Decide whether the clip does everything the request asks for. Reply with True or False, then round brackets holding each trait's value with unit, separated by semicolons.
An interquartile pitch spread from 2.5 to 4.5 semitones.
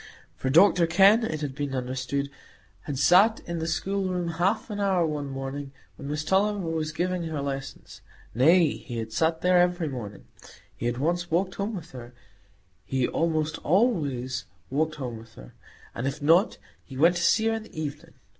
False (4.9 semitones)